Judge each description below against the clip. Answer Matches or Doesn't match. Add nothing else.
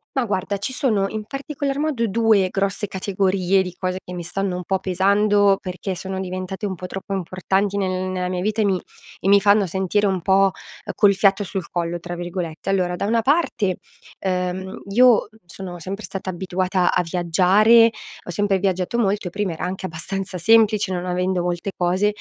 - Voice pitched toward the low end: Doesn't match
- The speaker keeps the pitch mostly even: Matches